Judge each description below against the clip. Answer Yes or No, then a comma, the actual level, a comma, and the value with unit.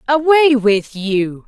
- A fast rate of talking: No, slow, 120 wpm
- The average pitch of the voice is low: No, high, 245 Hz